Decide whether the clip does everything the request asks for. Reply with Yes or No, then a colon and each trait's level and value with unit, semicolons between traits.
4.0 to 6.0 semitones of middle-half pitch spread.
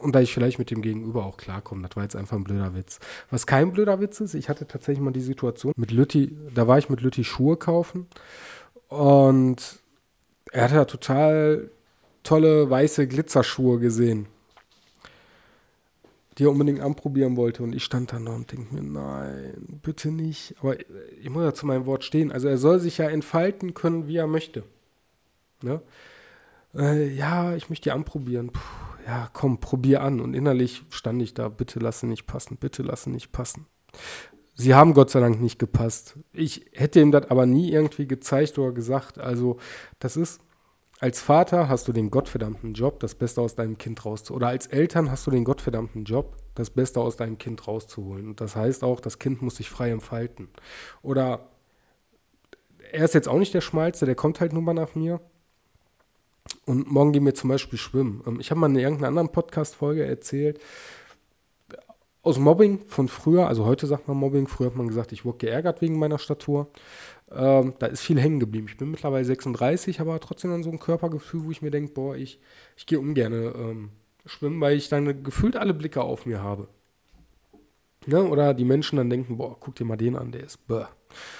Yes: average, 4.3 semitones